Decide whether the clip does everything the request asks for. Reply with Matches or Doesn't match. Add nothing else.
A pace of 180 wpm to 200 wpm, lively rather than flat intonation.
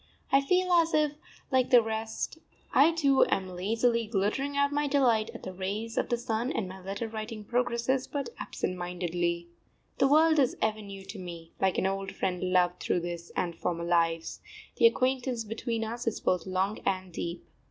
Matches